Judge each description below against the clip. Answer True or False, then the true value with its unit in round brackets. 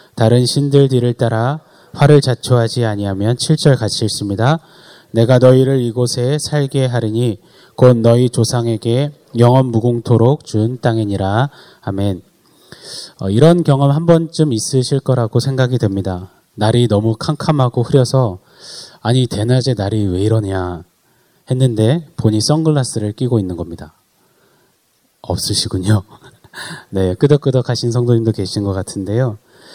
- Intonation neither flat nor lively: True (3.7 semitones)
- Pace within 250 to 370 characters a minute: True (280 characters per minute)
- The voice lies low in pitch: True (120 Hz)